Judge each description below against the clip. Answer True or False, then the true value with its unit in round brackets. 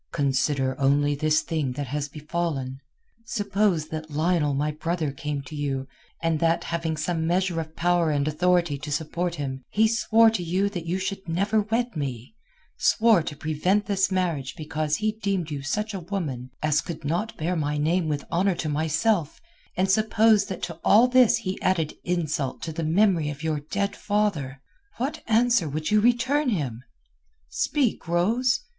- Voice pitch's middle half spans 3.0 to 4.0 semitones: False (5.1 semitones)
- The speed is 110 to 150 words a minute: False (175 wpm)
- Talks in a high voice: False (165 Hz)